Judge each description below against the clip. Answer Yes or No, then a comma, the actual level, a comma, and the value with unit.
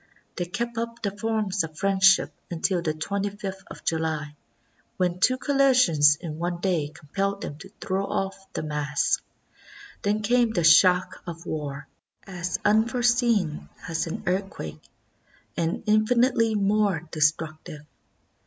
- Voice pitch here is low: No, high, 190 Hz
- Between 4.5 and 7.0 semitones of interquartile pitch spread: Yes, average, 4.8 semitones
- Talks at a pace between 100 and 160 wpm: Yes, slow, 135 wpm